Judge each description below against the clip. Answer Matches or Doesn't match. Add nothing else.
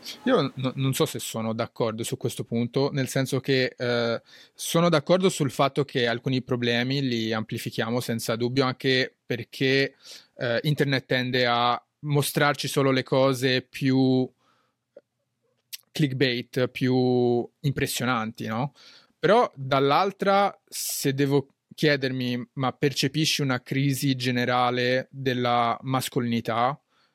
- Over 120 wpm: Doesn't match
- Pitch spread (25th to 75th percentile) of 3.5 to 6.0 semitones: Doesn't match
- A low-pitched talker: Matches